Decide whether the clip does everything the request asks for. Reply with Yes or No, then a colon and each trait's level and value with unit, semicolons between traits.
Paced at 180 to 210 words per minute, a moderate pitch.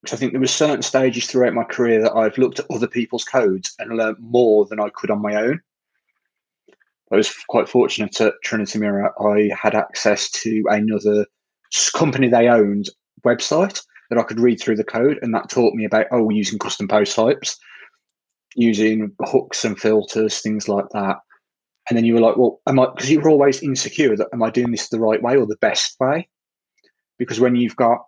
No: average, 200 wpm; low, 115 Hz